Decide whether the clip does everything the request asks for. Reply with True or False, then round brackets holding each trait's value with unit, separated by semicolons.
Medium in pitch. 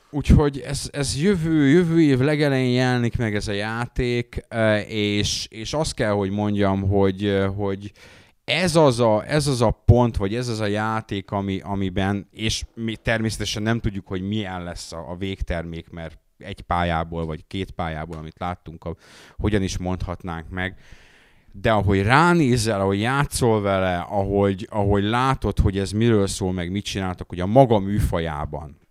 False (100 Hz)